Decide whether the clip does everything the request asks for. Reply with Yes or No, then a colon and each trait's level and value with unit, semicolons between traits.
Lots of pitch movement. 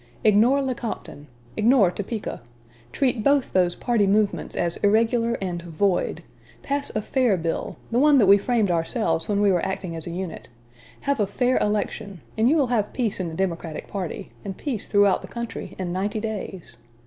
No: average, 4.3 semitones